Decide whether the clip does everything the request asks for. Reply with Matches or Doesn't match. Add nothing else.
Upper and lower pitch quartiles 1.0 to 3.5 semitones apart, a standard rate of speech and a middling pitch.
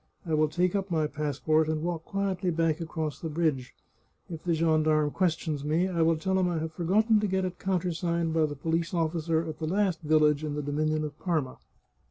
Doesn't match